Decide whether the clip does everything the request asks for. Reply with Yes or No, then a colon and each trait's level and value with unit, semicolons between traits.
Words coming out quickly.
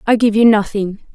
Yes: fast, 210 wpm